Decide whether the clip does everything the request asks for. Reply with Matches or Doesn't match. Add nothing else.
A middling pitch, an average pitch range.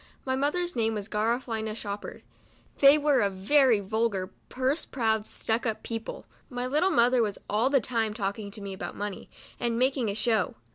Doesn't match